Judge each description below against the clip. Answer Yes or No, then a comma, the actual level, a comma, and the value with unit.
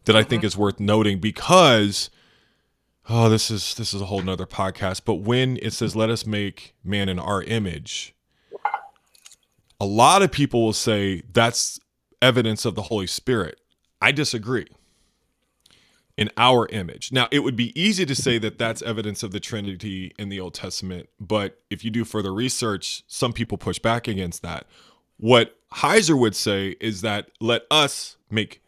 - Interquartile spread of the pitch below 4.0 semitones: Yes, average, 2.8 semitones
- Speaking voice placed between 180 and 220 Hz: No, low, 110 Hz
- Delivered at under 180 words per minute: Yes, average, 170 wpm